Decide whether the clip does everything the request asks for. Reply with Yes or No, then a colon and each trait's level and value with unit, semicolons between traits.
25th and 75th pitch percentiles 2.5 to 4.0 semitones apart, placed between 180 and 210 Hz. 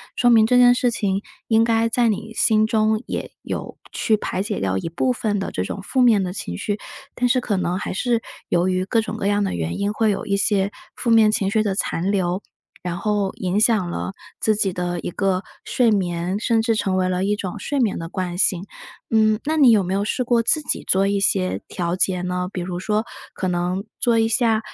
Yes: average, 3.4 semitones; high, 205 Hz